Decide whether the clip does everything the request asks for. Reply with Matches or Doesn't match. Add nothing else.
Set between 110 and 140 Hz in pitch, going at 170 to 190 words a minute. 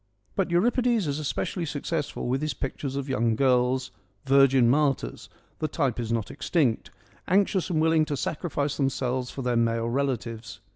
Matches